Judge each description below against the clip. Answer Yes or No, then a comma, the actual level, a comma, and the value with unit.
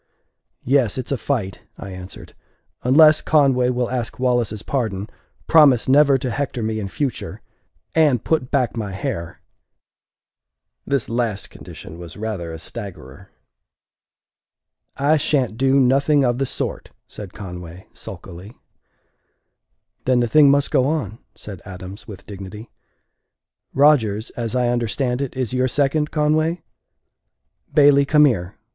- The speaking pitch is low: Yes, low, 125 Hz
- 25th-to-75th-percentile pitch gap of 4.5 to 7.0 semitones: Yes, average, 5.2 semitones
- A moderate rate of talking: No, slow, 130 wpm